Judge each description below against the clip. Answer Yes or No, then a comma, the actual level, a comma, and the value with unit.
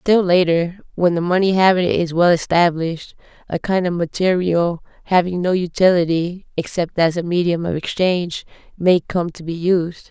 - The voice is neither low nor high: Yes, medium, 175 Hz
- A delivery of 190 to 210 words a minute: No, average, 160 wpm